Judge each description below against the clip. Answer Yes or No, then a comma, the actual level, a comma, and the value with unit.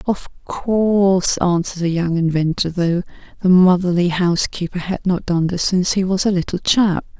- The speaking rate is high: No, average, 165 wpm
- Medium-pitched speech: Yes, medium, 180 Hz